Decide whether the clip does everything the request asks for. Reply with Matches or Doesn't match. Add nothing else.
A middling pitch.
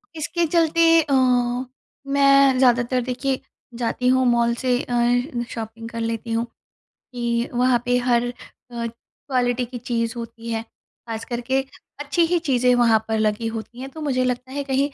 Doesn't match